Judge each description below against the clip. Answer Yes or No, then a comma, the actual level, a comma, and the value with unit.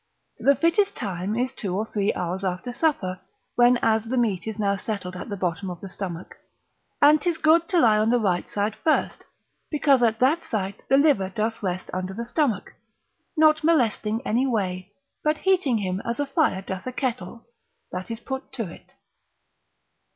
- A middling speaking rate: Yes, average, 185 wpm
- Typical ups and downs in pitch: No, wide, 6.1 semitones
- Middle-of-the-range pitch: No, high, 225 Hz